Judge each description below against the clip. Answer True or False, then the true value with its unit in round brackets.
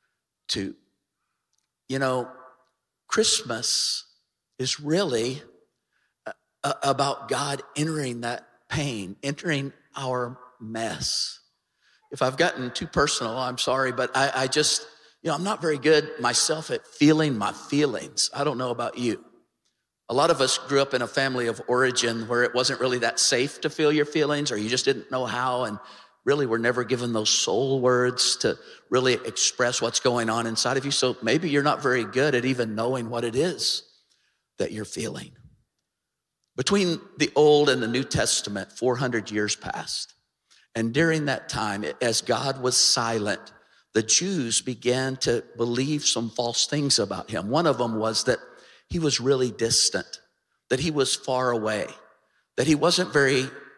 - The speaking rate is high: False (165 wpm)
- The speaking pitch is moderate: False (130 Hz)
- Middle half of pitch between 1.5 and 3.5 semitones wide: True (3.0 semitones)